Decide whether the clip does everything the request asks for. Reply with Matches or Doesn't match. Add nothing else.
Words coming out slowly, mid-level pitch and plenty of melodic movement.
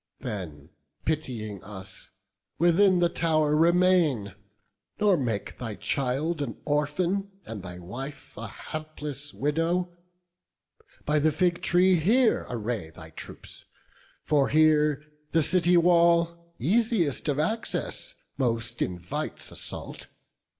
Matches